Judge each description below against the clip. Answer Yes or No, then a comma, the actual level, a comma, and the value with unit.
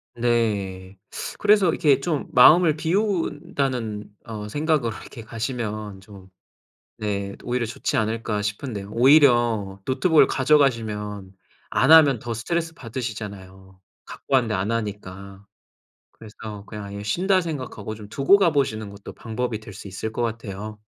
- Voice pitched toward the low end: Yes, low, 115 Hz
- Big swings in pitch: No, average, 5.0 semitones